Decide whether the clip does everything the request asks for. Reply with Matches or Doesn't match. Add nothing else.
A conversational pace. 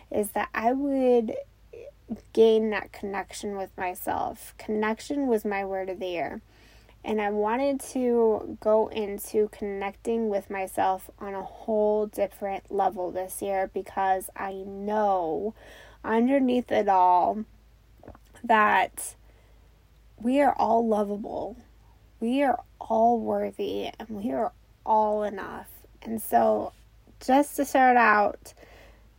Doesn't match